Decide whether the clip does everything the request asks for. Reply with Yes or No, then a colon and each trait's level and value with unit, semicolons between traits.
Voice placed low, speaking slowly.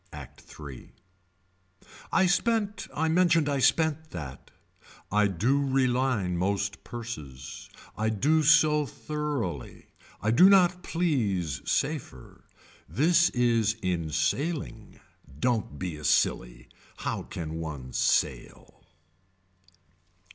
Yes: low, 120 Hz; slow, 105 wpm